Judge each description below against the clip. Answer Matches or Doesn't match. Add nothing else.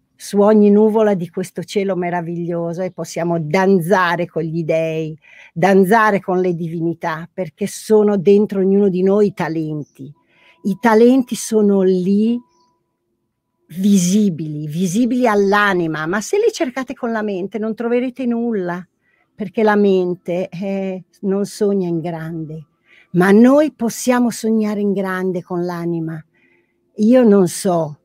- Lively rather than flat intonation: Doesn't match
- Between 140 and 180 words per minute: Doesn't match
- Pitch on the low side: Doesn't match